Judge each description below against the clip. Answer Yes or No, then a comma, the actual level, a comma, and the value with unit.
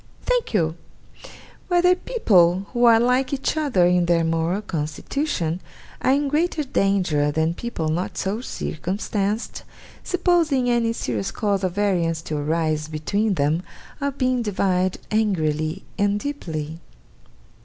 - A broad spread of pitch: Yes, wide, 7.4 semitones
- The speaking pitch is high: Yes, high, 195 Hz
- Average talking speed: No, slow, 130 wpm